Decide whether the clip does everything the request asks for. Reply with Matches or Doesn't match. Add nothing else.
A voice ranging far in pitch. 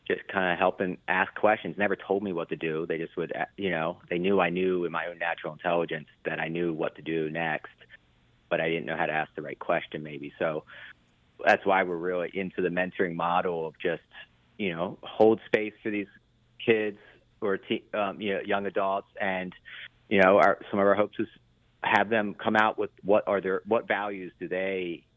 Doesn't match